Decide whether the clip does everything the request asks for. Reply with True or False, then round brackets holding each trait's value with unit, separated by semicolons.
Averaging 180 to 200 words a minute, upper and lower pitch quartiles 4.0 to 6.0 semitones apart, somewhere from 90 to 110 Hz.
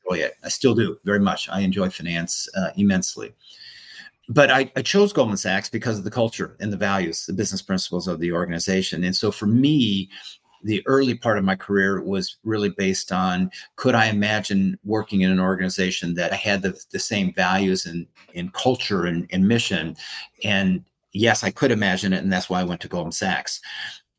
False (195 wpm; 2.5 semitones; 95 Hz)